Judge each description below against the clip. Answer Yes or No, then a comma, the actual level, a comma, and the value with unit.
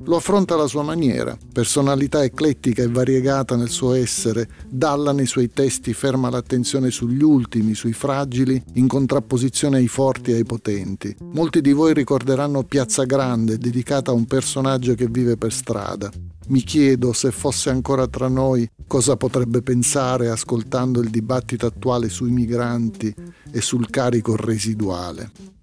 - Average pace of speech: Yes, average, 150 wpm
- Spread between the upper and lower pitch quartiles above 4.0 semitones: No, narrow, 2.6 semitones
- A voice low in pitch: Yes, low, 125 Hz